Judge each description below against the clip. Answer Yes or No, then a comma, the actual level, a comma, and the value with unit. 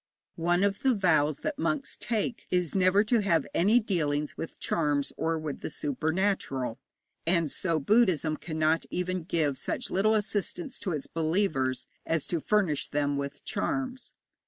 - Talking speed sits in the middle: Yes, average, 155 wpm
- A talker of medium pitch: Yes, medium, 170 Hz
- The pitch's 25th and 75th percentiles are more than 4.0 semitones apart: Yes, average, 5.1 semitones